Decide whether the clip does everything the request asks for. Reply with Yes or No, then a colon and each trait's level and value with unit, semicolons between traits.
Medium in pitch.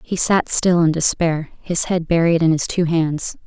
Yes: medium, 165 Hz